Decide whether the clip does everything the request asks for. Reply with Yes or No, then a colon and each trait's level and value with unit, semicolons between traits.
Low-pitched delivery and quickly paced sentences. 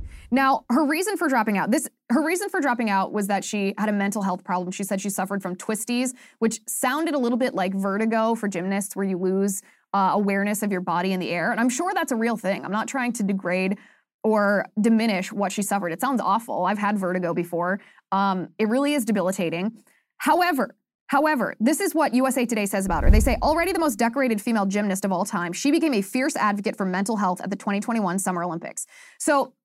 No: high, 210 Hz; fast, 225 wpm